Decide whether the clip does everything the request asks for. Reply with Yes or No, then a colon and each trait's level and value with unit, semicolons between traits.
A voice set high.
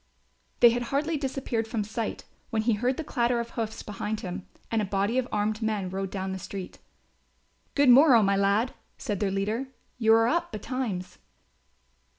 Yes: high, 220 Hz